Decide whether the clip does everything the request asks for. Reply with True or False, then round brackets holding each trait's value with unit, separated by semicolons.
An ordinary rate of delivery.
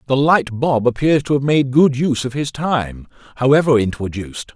True (185 wpm)